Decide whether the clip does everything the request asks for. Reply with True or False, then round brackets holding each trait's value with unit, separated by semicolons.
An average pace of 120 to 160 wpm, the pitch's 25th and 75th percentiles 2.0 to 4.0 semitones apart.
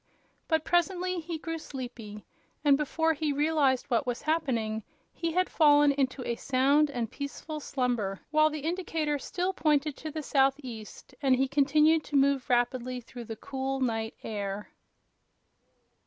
True (150 wpm; 3.7 semitones)